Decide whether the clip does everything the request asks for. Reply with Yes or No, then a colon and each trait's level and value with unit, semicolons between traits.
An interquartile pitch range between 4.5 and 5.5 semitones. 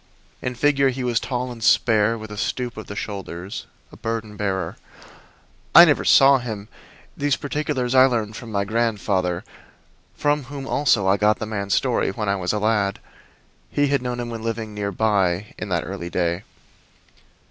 No: average, 3.8 semitones